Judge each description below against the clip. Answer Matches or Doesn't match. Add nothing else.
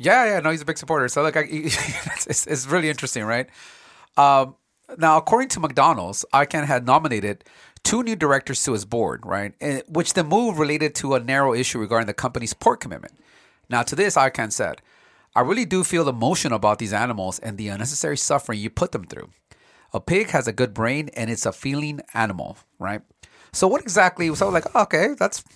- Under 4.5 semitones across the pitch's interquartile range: Doesn't match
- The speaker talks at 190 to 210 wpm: Matches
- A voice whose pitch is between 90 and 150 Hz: Matches